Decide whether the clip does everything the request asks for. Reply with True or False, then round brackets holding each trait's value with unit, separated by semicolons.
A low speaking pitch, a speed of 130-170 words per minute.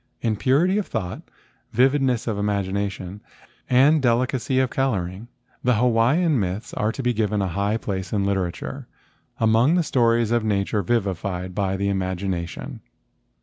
True (110 Hz; 150 wpm)